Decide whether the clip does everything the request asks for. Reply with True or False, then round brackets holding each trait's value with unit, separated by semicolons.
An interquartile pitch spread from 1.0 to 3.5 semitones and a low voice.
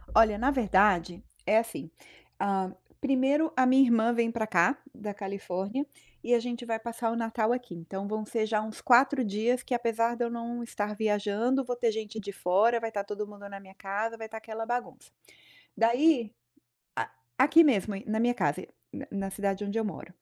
False (2.8 semitones; 225 Hz)